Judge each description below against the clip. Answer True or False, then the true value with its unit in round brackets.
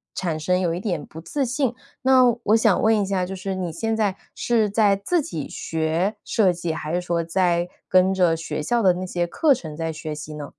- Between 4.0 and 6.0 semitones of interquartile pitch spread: True (4.4 semitones)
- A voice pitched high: False (180 Hz)